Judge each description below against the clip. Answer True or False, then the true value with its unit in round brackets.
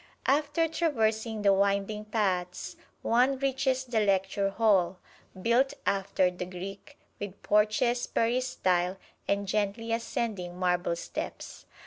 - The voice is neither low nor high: False (210 Hz)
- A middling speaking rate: False (110 wpm)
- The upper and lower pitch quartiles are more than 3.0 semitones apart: True (4.0 semitones)